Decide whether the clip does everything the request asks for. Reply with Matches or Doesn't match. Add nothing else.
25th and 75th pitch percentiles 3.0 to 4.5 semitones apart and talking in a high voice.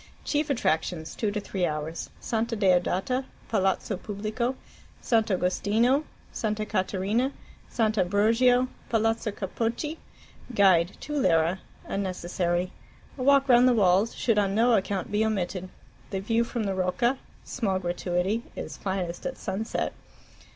Matches